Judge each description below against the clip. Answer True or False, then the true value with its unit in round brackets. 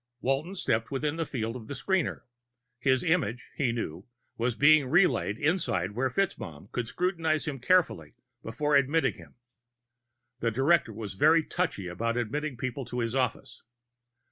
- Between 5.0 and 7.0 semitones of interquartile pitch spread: True (5.3 semitones)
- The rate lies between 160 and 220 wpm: False (150 wpm)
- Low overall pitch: True (130 Hz)